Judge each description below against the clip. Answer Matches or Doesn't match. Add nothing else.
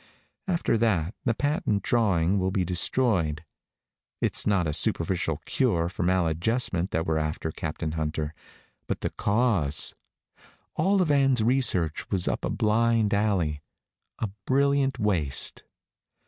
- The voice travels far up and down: Matches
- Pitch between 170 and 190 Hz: Doesn't match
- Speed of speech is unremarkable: Doesn't match